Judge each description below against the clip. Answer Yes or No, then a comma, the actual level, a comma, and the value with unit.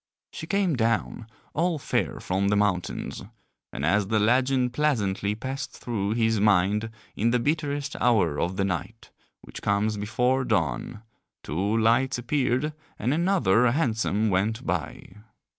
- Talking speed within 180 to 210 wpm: No, average, 140 wpm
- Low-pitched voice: Yes, low, 110 Hz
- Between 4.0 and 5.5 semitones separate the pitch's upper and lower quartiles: Yes, average, 4.5 semitones